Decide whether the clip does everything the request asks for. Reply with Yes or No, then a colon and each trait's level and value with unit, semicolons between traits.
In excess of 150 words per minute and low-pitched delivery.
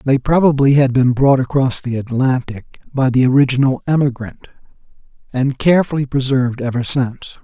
No: slow, 135 wpm; low, 130 Hz